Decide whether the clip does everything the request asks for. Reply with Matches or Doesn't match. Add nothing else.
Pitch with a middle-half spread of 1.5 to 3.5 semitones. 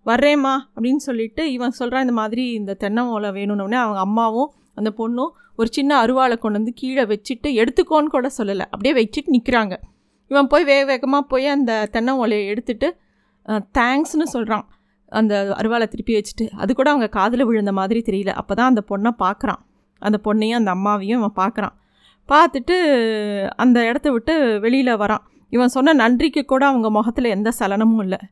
Doesn't match